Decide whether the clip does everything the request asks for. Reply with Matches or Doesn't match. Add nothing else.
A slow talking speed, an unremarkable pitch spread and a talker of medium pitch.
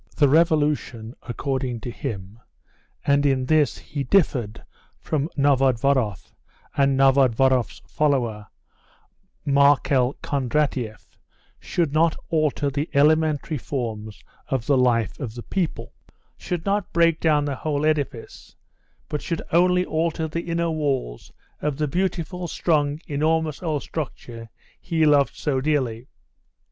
Matches